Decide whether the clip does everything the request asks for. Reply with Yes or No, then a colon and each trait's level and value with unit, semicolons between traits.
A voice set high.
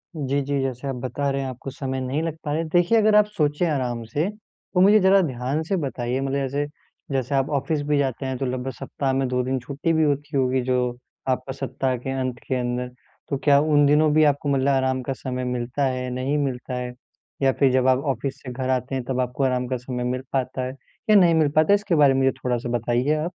No: low, 135 Hz